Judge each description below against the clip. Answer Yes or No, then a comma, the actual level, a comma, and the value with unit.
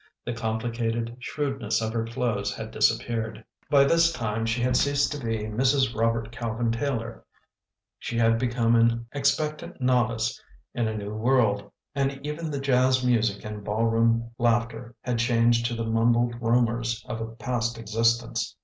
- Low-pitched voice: Yes, low, 115 Hz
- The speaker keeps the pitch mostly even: Yes, narrow, 1.7 semitones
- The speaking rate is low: No, average, 160 wpm